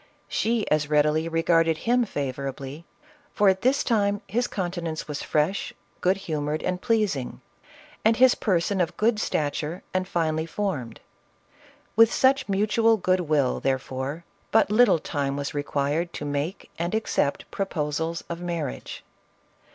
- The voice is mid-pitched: Yes, medium, 170 Hz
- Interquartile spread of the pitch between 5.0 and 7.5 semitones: Yes, wide, 5.5 semitones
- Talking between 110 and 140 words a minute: Yes, slow, 135 wpm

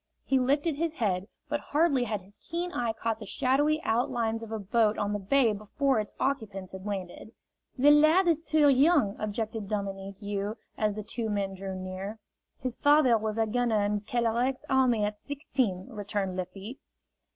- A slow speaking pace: No, average, 175 wpm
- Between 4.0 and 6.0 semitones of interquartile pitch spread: Yes, average, 4.9 semitones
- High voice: Yes, high, 225 Hz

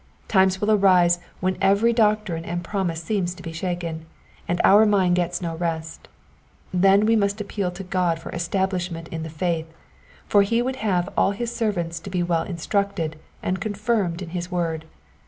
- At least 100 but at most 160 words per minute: No, average, 180 wpm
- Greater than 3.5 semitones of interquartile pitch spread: No, average, 3.0 semitones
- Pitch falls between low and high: Yes, medium, 180 Hz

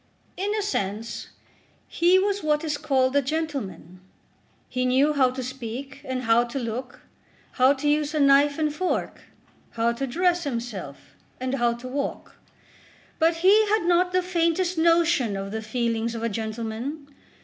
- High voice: Yes, very high, 275 Hz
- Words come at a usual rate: Yes, average, 160 wpm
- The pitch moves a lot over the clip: Yes, wide, 5.8 semitones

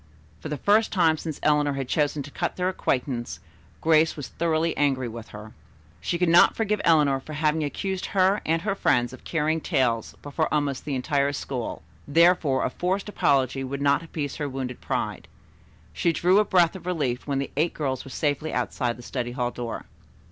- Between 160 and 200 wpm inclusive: Yes, average, 190 wpm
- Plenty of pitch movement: No, average, 4.0 semitones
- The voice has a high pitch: No, medium, 145 Hz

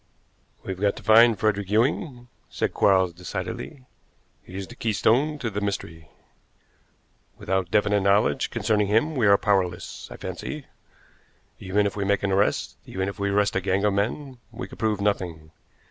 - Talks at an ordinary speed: Yes, average, 165 wpm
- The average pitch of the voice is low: Yes, low, 100 Hz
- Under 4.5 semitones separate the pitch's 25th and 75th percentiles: Yes, narrow, 2.5 semitones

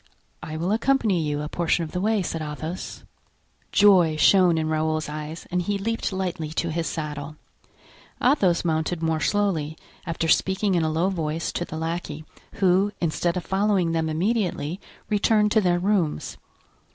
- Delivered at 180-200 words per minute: No, average, 165 wpm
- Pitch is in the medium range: Yes, medium, 170 Hz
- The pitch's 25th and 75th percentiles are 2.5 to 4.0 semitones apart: Yes, average, 3.7 semitones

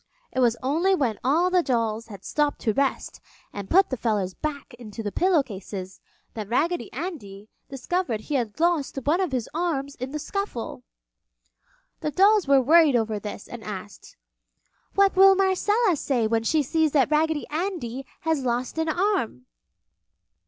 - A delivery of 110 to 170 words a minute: Yes, average, 165 wpm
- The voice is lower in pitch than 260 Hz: No, very high, 275 Hz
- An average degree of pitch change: No, wide, 7.0 semitones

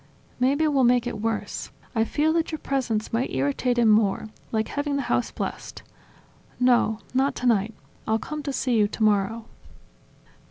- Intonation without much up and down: No, average, 4.0 semitones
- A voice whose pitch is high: Yes, high, 240 Hz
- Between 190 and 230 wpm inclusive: No, average, 160 wpm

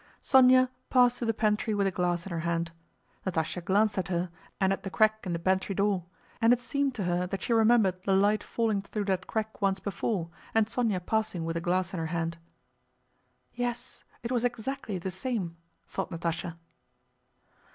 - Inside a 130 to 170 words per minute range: No, average, 190 wpm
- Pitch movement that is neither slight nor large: Yes, average, 4.1 semitones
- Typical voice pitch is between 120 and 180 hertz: No, high, 195 Hz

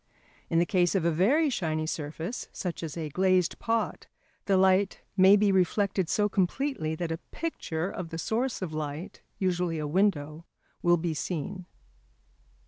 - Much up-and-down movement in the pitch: No, average, 3.5 semitones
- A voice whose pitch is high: No, medium, 180 Hz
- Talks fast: No, average, 160 wpm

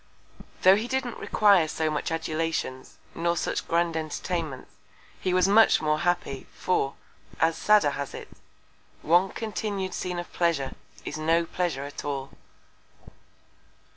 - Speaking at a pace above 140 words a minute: No, slow, 135 wpm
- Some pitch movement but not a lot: Yes, average, 3.3 semitones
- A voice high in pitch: No, medium, 170 Hz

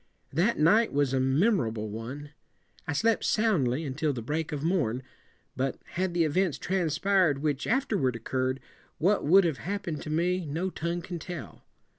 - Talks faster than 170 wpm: Yes, average, 185 wpm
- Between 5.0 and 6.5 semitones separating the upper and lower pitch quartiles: Yes, wide, 5.6 semitones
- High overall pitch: No, medium, 155 Hz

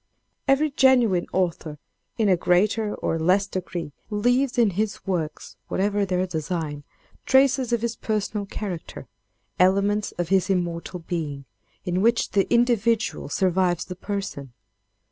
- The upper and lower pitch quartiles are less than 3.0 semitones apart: No, average, 3.9 semitones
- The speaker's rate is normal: No, slow, 130 wpm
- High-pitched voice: Yes, high, 195 Hz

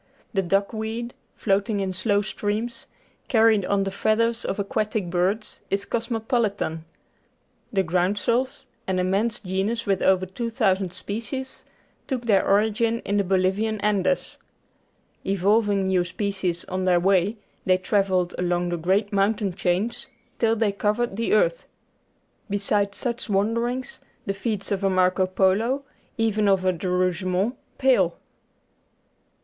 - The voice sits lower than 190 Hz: No, high, 200 Hz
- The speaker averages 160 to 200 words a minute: No, slow, 135 wpm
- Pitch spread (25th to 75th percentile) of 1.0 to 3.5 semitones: Yes, average, 3.1 semitones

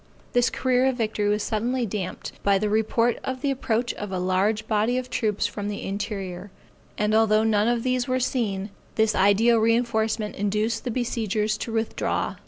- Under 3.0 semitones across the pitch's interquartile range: Yes, narrow, 2.5 semitones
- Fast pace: No, average, 180 wpm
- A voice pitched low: No, high, 220 Hz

